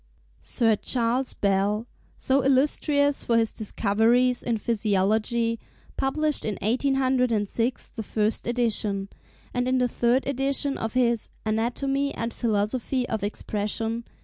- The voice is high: Yes, high, 235 Hz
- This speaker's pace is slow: Yes, slow, 120 wpm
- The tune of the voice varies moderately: Yes, average, 3.1 semitones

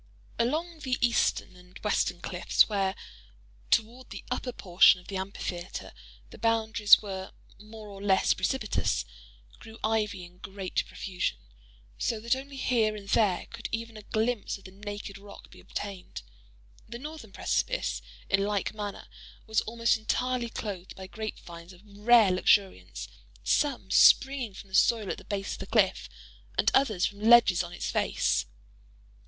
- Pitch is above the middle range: Yes, high, 205 Hz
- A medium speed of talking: Yes, average, 150 wpm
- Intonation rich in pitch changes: No, average, 3.5 semitones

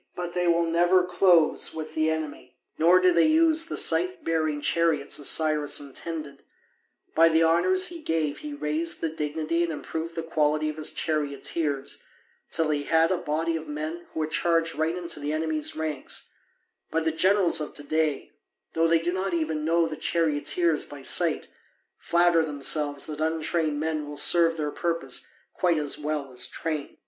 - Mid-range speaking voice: Yes, medium, 160 Hz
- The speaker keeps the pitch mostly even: Yes, narrow, 1.9 semitones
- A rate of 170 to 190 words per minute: Yes, average, 175 wpm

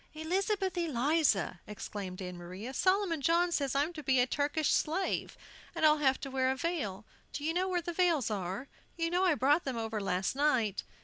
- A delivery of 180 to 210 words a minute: Yes, average, 195 wpm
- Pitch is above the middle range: Yes, very high, 285 Hz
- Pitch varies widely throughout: Yes, wide, 6.9 semitones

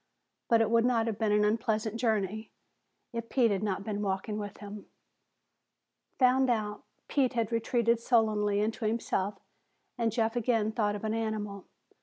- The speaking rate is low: No, average, 160 wpm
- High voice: Yes, high, 220 Hz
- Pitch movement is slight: Yes, narrow, 1.9 semitones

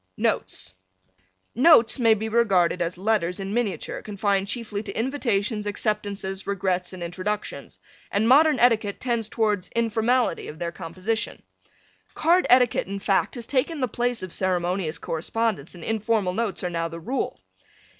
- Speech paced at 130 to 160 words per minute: Yes, average, 145 wpm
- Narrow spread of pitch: No, average, 3.9 semitones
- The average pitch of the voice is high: Yes, high, 210 Hz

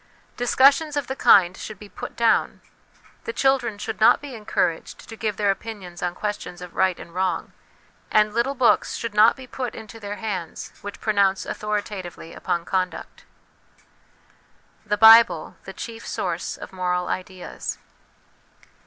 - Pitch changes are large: No, average, 3.7 semitones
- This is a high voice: Yes, high, 210 Hz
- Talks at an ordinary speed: Yes, average, 150 wpm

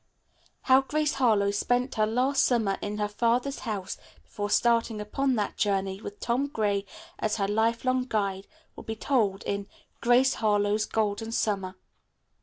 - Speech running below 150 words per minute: No, average, 155 wpm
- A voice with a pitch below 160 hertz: No, high, 220 Hz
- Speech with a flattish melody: No, average, 3.2 semitones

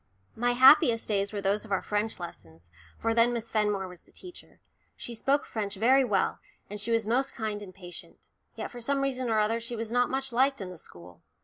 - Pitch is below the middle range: No, high, 225 Hz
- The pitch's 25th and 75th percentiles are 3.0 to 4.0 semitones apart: Yes, average, 3.4 semitones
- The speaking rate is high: Yes, fast, 220 wpm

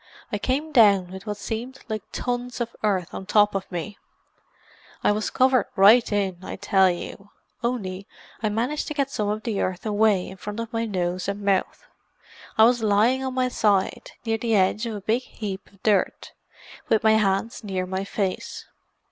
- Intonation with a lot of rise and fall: No, average, 3.0 semitones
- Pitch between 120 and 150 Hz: No, high, 210 Hz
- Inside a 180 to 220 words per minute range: Yes, average, 190 wpm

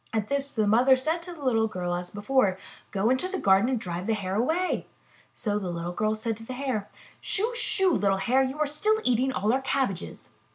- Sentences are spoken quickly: Yes, fast, 220 wpm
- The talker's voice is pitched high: Yes, high, 235 Hz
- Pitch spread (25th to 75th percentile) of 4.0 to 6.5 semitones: Yes, average, 5.3 semitones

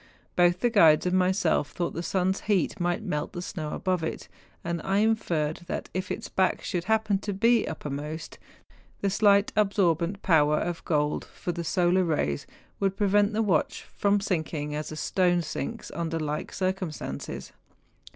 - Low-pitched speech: No, medium, 180 Hz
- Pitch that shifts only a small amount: No, average, 3.8 semitones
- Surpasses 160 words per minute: Yes, average, 170 wpm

